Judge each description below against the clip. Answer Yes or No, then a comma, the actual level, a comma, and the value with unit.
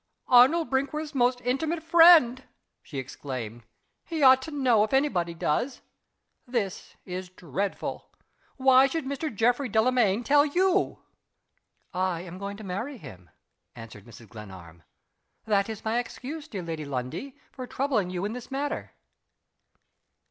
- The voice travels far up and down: Yes, wide, 7.5 semitones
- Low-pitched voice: No, high, 240 Hz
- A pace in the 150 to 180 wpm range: No, average, 140 wpm